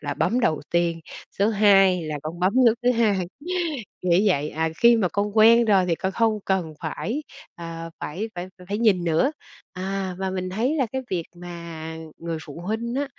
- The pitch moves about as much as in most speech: Yes, average, 4.6 semitones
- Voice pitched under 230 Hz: Yes, high, 190 Hz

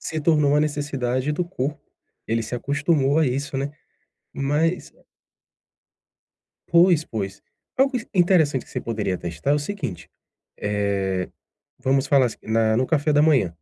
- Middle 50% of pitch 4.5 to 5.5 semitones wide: Yes, average, 5.1 semitones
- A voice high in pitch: No, medium, 140 Hz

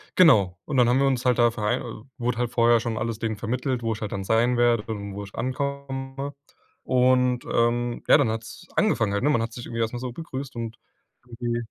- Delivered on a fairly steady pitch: Yes, narrow, 2.3 semitones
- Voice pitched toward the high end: No, low, 120 Hz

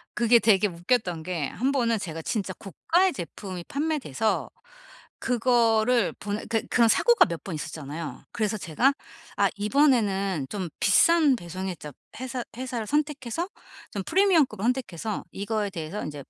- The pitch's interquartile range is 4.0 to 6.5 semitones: Yes, wide, 5.5 semitones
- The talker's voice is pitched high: Yes, high, 220 Hz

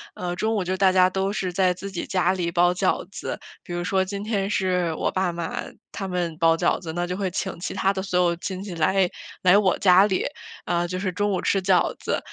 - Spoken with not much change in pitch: Yes, narrow, 1.5 semitones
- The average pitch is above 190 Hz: No, medium, 185 Hz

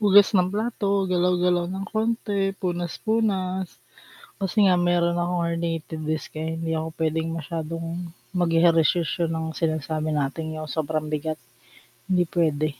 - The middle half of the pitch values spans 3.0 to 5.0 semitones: No, narrow, 2.5 semitones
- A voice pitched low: No, medium, 170 Hz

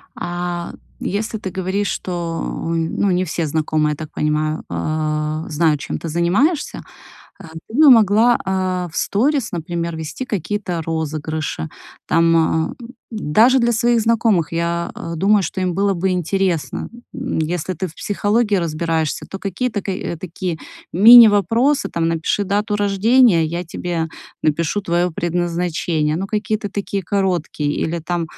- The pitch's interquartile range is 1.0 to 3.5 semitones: No, average, 4.0 semitones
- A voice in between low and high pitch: Yes, medium, 175 Hz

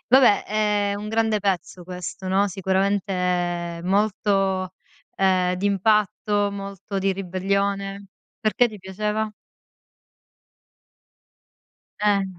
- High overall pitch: Yes, high, 195 Hz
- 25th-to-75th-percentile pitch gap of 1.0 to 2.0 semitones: Yes, narrow, 1.7 semitones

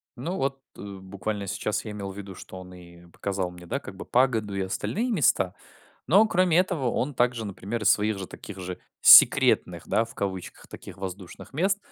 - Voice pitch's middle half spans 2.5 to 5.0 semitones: No, wide, 5.5 semitones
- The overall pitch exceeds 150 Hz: No, low, 100 Hz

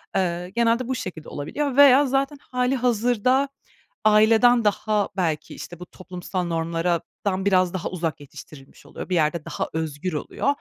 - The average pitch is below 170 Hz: No, high, 190 Hz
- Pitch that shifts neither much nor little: No, wide, 6.5 semitones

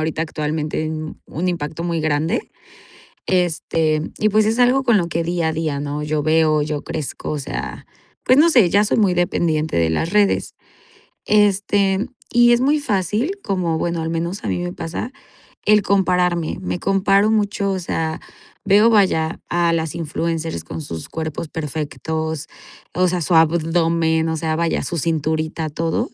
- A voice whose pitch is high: No, medium, 165 Hz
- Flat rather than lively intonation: No, average, 3.8 semitones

